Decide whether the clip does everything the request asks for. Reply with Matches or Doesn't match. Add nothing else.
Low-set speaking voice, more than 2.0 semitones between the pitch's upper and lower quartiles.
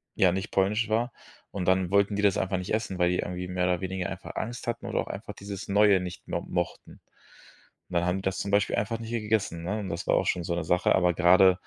Matches